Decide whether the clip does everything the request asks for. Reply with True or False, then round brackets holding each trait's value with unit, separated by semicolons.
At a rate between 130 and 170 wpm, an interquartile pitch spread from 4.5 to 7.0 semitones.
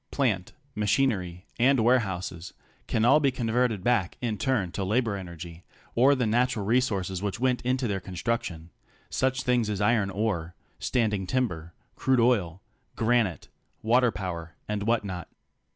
True (145 wpm; 4.8 semitones)